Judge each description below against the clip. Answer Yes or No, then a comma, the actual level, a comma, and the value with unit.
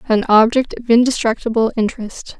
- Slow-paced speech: Yes, slow, 125 wpm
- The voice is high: Yes, high, 230 Hz